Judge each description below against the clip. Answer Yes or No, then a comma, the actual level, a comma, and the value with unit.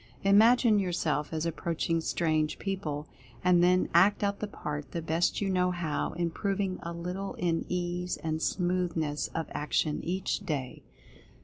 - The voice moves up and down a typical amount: Yes, average, 3.0 semitones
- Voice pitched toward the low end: No, medium, 175 Hz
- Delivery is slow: No, average, 155 wpm